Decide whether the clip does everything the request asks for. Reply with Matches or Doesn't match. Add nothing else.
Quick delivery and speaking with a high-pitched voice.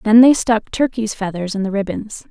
Matches